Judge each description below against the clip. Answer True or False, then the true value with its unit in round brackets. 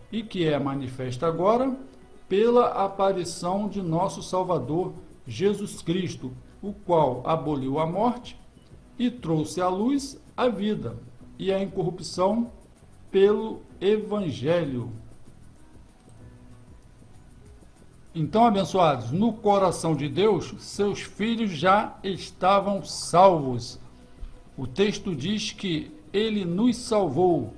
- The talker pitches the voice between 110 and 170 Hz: False (185 Hz)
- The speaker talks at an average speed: False (100 wpm)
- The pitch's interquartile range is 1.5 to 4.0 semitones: False (4.7 semitones)